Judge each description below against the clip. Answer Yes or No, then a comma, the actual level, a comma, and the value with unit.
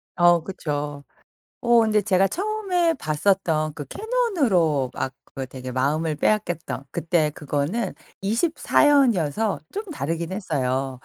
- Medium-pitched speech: Yes, medium, 175 Hz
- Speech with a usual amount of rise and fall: No, wide, 7.9 semitones